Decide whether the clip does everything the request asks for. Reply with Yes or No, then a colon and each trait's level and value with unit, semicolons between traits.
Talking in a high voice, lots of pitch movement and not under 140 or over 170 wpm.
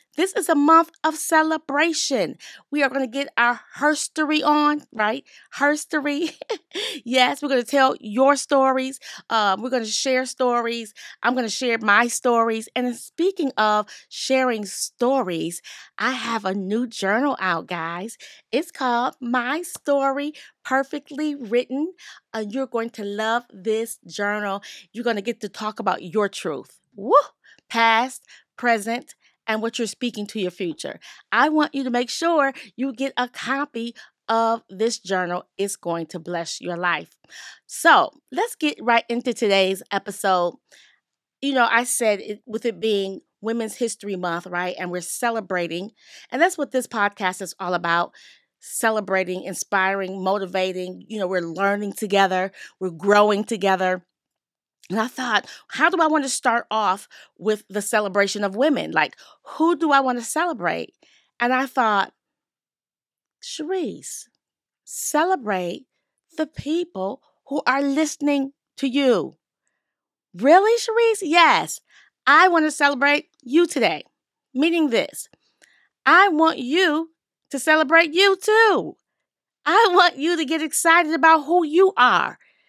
Yes: high, 245 Hz; wide, 6.5 semitones; average, 145 wpm